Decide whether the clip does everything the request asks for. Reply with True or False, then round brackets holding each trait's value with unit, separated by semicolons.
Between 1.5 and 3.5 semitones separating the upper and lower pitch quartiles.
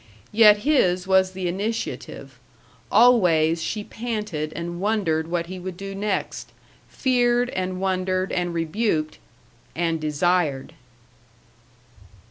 False (4.0 semitones)